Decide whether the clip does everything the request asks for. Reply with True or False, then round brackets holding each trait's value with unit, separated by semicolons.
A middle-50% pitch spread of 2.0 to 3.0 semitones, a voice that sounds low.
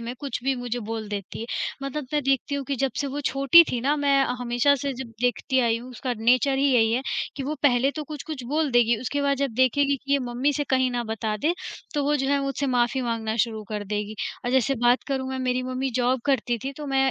False (2.6 semitones; 260 Hz)